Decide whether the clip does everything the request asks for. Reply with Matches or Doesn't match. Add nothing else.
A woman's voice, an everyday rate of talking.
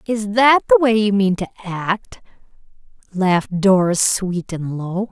Matches